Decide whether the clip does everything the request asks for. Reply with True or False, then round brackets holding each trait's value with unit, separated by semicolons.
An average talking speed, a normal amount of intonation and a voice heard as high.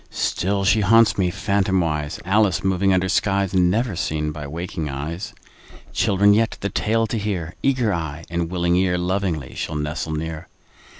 False (160 wpm; 3.6 semitones; 90 Hz)